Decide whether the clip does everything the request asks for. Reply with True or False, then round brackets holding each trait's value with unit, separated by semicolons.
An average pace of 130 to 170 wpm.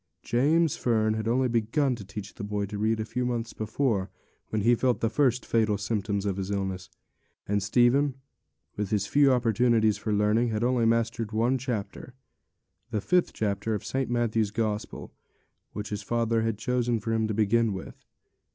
False (180 wpm)